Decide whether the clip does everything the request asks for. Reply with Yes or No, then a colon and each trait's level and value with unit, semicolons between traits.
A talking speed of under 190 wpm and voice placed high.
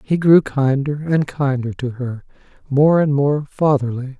No: average, 155 wpm; medium, 140 Hz